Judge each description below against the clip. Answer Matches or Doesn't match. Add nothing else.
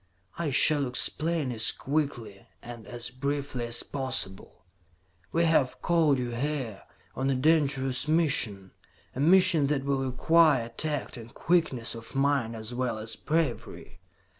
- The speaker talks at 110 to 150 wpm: Matches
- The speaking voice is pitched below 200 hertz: Matches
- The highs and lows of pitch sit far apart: Doesn't match